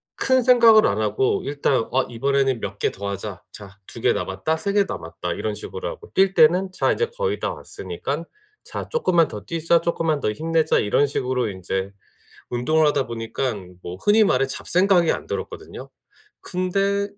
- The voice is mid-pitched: Yes, medium, 155 Hz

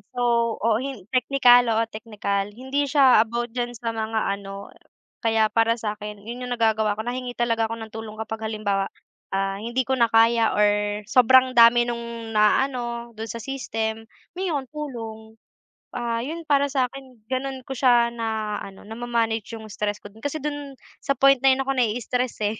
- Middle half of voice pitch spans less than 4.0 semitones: Yes, narrow, 2.5 semitones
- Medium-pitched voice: No, high, 230 Hz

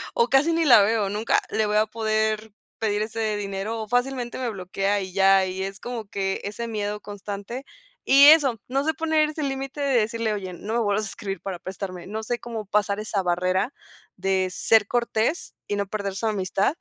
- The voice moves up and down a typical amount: Yes, average, 3.3 semitones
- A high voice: Yes, high, 215 Hz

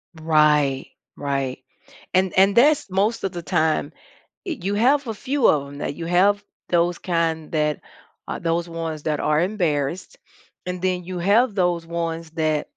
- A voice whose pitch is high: No, medium, 170 Hz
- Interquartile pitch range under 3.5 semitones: No, average, 3.9 semitones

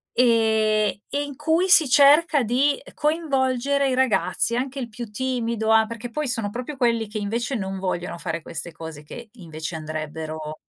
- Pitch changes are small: No, wide, 5.7 semitones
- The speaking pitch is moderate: No, high, 235 Hz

